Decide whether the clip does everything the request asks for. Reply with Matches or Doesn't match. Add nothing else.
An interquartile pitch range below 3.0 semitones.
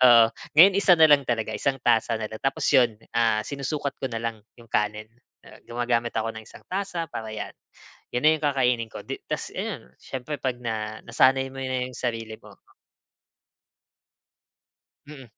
Doesn't match